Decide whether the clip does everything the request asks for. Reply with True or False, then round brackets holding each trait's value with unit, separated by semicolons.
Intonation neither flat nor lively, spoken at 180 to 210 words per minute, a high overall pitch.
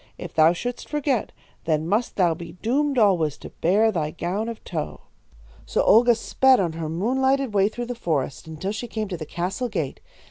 False (6.4 semitones; 200 wpm; 200 Hz)